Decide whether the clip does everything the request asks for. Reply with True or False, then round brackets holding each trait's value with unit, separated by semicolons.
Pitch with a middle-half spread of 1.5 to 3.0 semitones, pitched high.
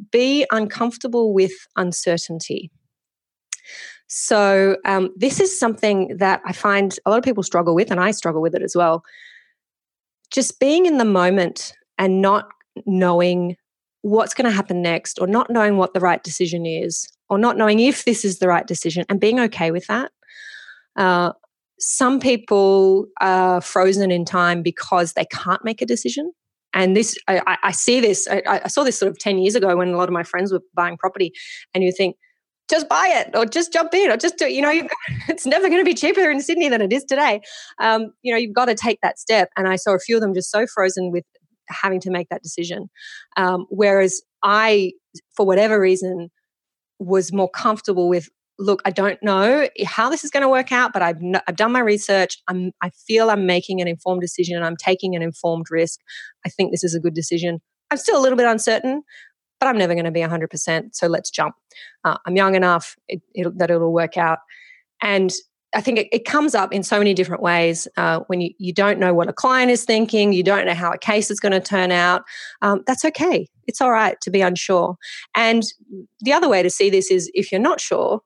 False (4.5 semitones; 195 Hz)